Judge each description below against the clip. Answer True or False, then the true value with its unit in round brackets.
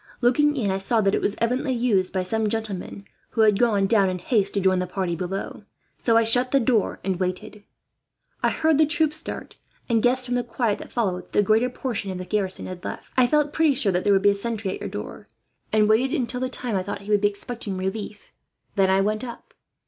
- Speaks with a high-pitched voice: True (215 Hz)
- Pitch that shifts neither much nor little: True (4.1 semitones)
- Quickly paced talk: True (245 wpm)